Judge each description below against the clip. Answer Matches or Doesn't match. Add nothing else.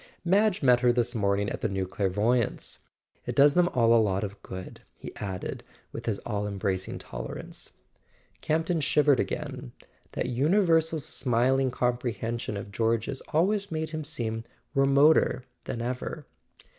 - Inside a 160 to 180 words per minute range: Doesn't match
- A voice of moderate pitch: Doesn't match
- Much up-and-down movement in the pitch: Matches